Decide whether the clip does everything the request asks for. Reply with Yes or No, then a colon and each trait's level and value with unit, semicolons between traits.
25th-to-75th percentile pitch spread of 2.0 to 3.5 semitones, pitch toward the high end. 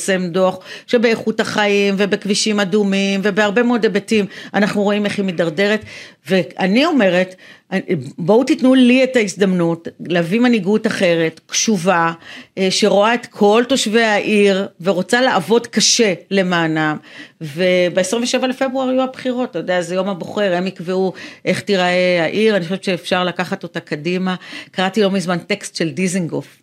Yes: average, 3.2 semitones; high, 195 Hz